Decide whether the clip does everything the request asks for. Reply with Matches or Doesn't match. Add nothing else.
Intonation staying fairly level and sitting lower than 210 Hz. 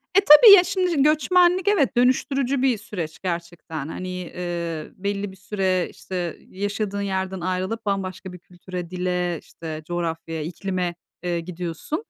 Doesn't match